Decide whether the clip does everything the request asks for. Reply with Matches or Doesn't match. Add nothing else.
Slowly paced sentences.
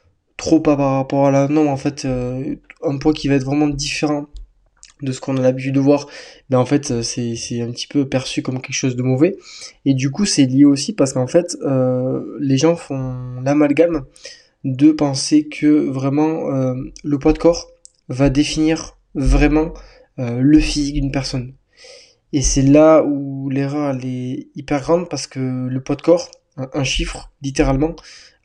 Doesn't match